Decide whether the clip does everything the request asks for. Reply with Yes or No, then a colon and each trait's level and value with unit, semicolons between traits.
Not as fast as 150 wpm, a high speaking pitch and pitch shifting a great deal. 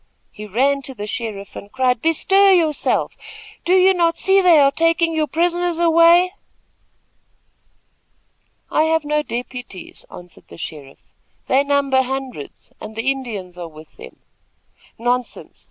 Yes: average, 140 wpm; very high, 275 Hz; wide, 6.6 semitones